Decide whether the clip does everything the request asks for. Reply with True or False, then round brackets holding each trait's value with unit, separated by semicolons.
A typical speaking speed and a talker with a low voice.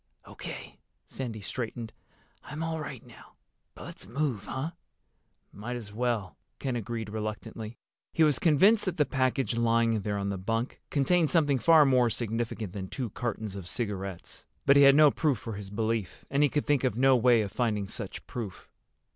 True (180 wpm; 120 Hz)